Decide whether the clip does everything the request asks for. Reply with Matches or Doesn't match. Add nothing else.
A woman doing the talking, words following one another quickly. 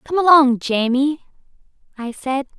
Doesn't match